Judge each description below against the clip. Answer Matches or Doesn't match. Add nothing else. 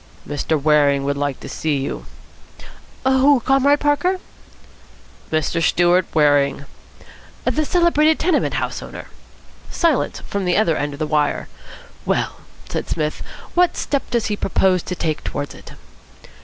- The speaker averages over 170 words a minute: Doesn't match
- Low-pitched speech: Doesn't match